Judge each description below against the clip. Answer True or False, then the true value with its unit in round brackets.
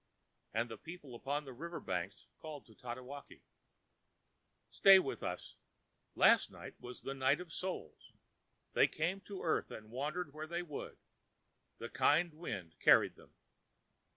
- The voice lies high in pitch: False (145 Hz)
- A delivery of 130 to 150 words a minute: True (145 wpm)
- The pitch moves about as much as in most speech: False (5.8 semitones)